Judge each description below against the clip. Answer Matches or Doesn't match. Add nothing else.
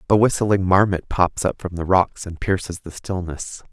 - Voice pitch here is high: Doesn't match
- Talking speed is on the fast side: Doesn't match